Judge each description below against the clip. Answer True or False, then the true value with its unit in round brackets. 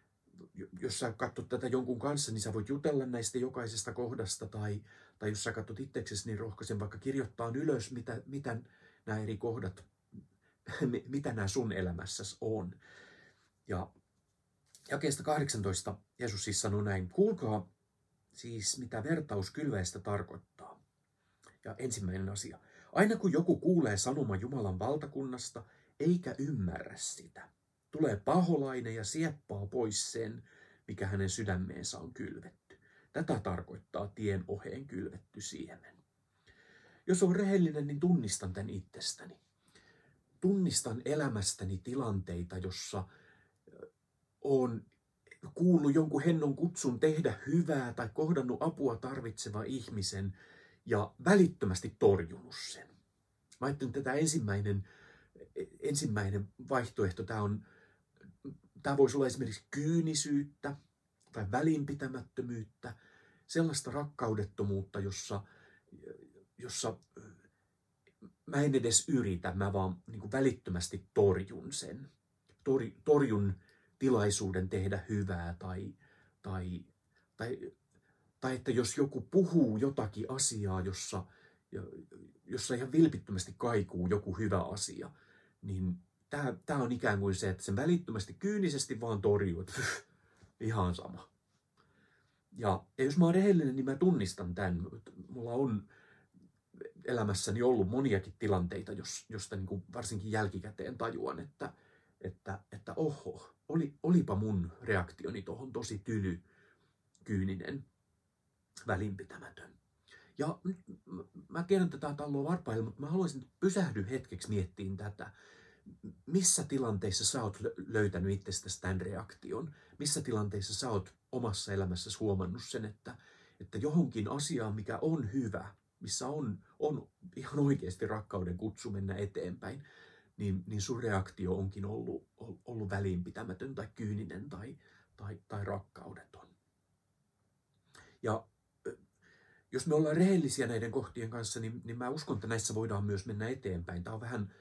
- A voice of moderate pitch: False (110 Hz)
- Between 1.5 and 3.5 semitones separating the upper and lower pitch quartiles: False (5.6 semitones)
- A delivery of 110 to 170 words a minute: True (115 wpm)